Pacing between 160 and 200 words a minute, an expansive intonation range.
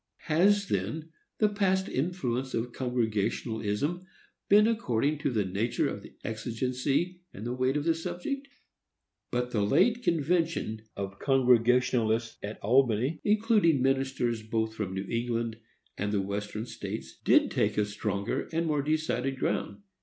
No: average, 140 wpm; wide, 6.6 semitones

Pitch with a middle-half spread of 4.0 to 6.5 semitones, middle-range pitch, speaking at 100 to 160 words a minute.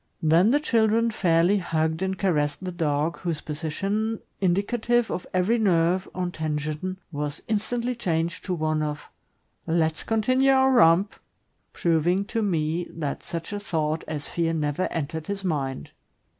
Yes: average, 4.6 semitones; medium, 175 Hz; average, 145 wpm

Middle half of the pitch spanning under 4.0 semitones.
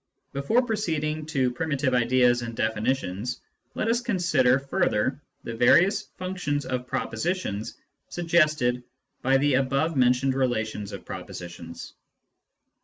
No: average, 4.6 semitones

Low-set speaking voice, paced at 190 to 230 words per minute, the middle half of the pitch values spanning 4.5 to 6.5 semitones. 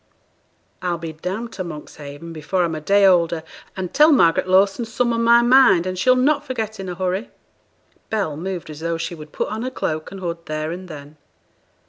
No: medium, 185 Hz; average, 200 wpm; average, 5.0 semitones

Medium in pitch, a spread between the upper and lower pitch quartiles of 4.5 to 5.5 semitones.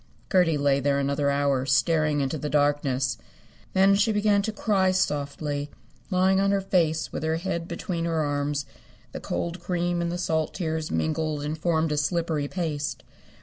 No: medium, 160 Hz; average, 3.5 semitones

